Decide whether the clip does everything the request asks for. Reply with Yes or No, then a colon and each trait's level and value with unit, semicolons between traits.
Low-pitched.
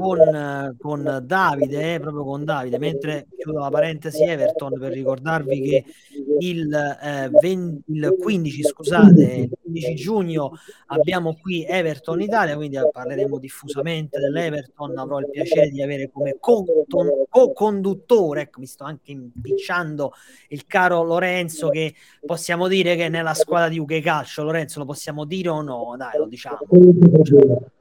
No: medium, 155 Hz